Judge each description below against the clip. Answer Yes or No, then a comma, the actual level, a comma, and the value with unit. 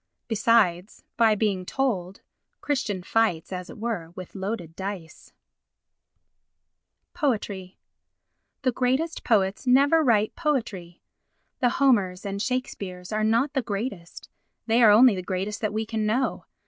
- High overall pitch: Yes, high, 215 Hz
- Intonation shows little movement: No, average, 4.6 semitones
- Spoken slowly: Yes, slow, 125 wpm